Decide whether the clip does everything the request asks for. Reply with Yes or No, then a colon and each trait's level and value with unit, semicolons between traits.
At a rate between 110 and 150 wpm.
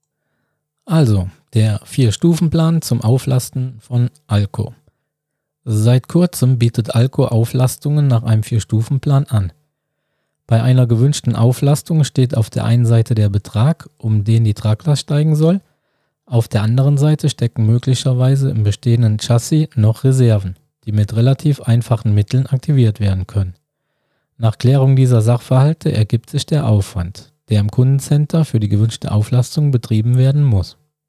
Yes: average, 140 wpm